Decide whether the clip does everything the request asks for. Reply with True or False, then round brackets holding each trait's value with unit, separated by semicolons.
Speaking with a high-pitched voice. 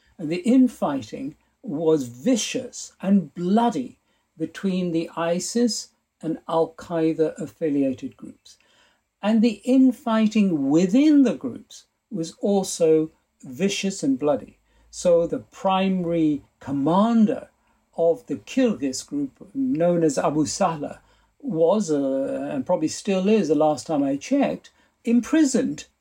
True (200 Hz)